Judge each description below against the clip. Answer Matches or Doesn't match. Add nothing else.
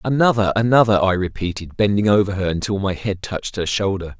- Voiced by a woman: Doesn't match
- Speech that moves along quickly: Doesn't match